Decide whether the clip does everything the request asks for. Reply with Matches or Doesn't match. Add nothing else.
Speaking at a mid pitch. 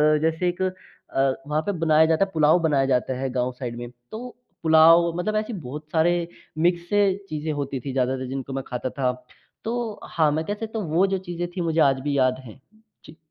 Matches